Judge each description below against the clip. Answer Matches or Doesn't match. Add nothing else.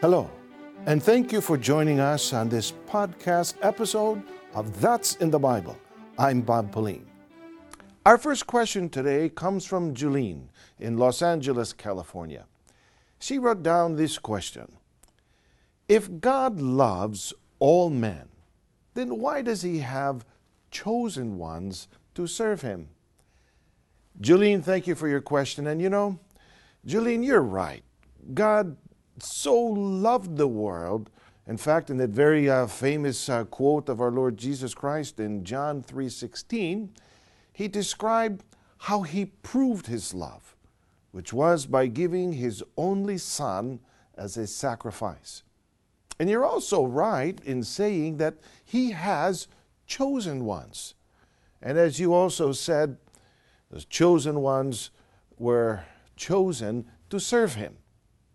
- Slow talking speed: Matches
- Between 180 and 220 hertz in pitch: Doesn't match